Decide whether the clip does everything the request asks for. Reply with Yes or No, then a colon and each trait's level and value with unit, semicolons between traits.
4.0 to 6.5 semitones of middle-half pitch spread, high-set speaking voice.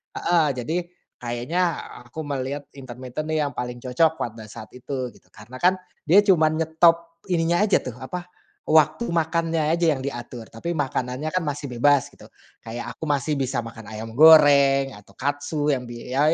No: average, 4.3 semitones; medium, 145 Hz